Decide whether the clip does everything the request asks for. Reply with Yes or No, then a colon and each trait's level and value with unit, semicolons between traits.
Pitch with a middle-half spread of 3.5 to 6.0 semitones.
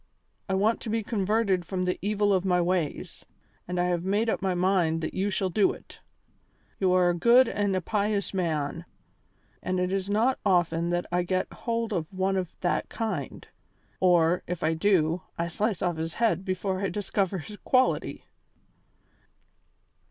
No: average, 2.8 semitones